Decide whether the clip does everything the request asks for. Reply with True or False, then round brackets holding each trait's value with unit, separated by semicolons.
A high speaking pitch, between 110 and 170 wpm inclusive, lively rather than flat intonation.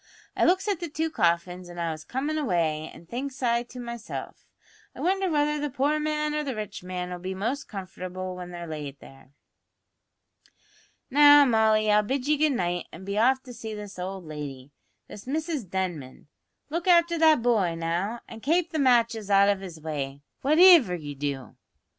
False (215 Hz; 185 wpm; 8.6 semitones)